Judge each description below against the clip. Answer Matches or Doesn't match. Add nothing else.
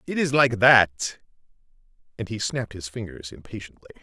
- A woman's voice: Doesn't match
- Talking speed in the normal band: Matches